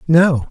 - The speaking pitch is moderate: Yes, medium, 155 Hz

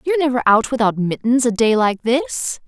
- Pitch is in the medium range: No, high, 240 Hz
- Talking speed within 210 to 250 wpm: No, average, 200 wpm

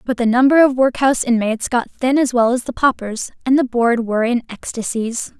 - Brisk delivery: Yes, fast, 210 wpm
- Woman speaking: Yes, female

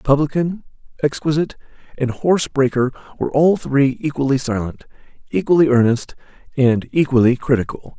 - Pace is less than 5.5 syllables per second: No, 5.6 syllables/s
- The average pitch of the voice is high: No, medium, 140 Hz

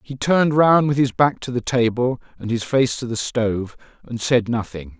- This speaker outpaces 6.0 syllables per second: No, 4.9 syllables/s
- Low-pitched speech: Yes, low, 125 Hz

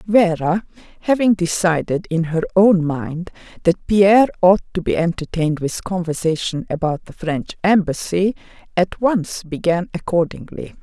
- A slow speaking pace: Yes, slow, 130 wpm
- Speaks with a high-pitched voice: No, medium, 180 Hz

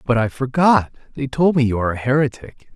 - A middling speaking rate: Yes, average, 195 wpm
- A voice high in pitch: No, low, 130 Hz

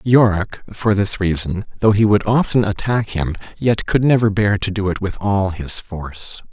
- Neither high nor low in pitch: No, low, 100 Hz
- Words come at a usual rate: Yes, average, 185 wpm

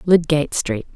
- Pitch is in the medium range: Yes, medium, 150 Hz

